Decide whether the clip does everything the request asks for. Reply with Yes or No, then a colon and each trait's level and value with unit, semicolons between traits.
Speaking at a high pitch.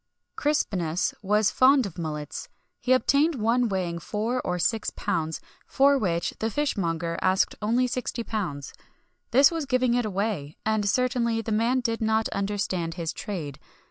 Yes: high, 215 Hz